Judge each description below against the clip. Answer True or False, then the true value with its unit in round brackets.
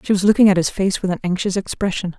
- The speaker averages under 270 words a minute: False (275 wpm)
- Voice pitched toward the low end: False (190 Hz)